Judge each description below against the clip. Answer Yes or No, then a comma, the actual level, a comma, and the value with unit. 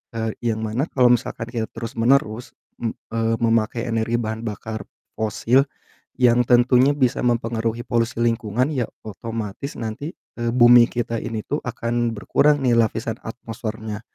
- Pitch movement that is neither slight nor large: No, narrow, 1.5 semitones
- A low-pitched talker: Yes, low, 115 Hz